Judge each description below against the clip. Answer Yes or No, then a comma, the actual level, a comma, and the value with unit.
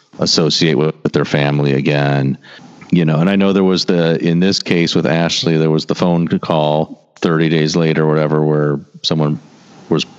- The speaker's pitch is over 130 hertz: No, very low, 80 Hz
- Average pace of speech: Yes, average, 185 wpm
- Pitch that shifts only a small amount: Yes, narrow, 2.1 semitones